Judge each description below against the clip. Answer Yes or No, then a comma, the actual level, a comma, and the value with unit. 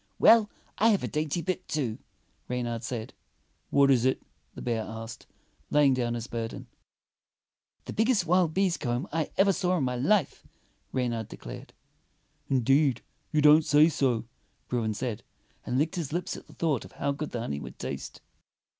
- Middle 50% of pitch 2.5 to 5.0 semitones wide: No, wide, 5.5 semitones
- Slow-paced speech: No, average, 170 wpm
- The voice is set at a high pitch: No, medium, 140 Hz